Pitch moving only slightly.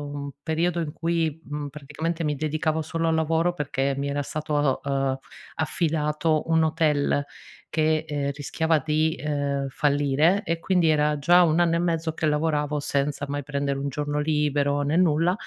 Yes: narrow, 2.1 semitones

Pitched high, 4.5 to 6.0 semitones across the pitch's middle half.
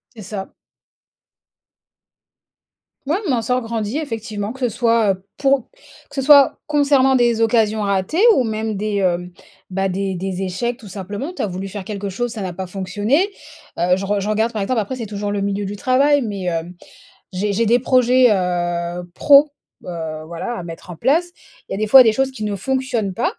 Yes: high, 215 Hz; average, 4.8 semitones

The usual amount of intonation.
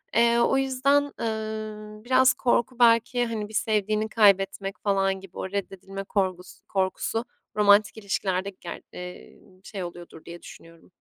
Yes: average, 3.0 semitones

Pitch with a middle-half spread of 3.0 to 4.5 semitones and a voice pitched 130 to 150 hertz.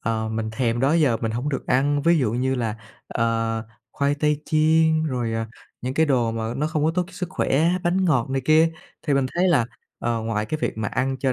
No: average, 5.3 semitones; low, 135 Hz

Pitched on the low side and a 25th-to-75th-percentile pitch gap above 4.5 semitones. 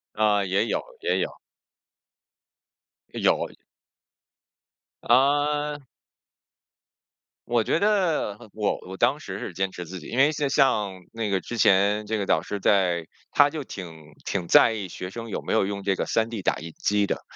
Yes: low, 105 Hz; average, 5.1 semitones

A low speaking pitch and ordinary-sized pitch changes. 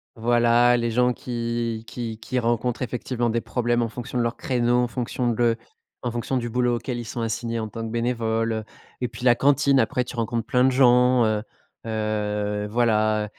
No: low, 120 Hz; narrow, 1.6 semitones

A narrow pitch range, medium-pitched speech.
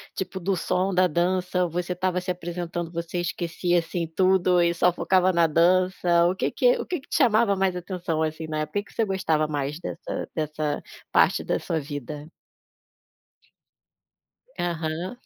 Yes: narrow, 2.2 semitones; medium, 175 Hz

